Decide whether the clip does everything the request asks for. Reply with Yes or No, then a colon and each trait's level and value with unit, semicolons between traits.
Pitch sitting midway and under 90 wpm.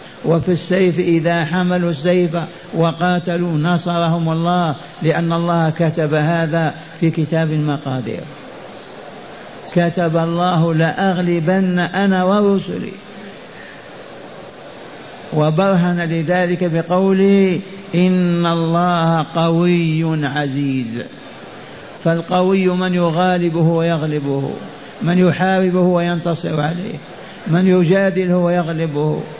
Yes: medium, 170 Hz; average, 80 wpm